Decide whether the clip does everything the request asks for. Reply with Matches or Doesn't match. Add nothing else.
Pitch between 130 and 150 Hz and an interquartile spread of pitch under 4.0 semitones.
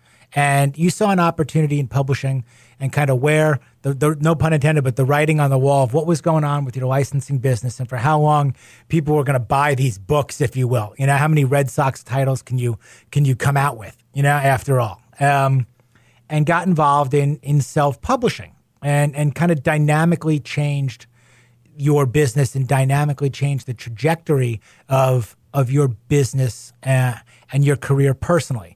Matches